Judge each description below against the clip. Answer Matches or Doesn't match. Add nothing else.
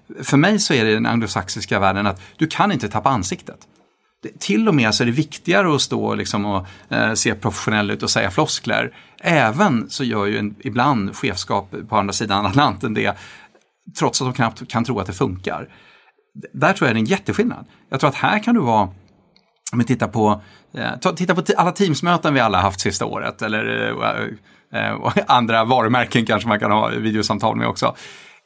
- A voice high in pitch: Doesn't match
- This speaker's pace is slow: Doesn't match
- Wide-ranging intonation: Matches